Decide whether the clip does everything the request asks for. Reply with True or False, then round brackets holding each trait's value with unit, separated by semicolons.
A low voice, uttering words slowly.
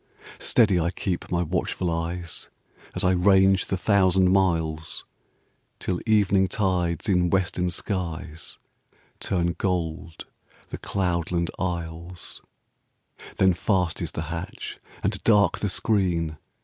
True (90 Hz; 115 wpm)